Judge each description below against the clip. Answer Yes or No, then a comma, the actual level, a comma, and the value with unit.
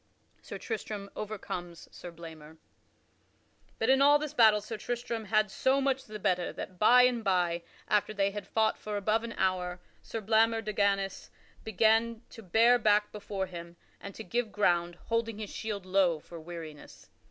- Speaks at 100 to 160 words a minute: No, average, 175 wpm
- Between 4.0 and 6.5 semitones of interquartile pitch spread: No, average, 3.6 semitones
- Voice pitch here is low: No, high, 210 Hz